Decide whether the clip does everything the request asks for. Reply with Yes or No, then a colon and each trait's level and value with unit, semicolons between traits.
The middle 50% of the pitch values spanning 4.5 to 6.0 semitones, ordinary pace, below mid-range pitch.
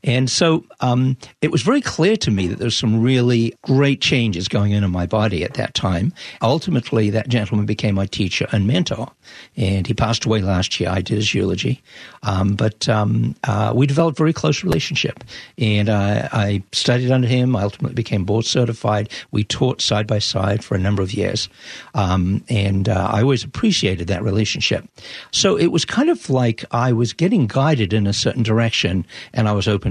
No: average, 4.0 semitones; average, 195 wpm; low, 110 Hz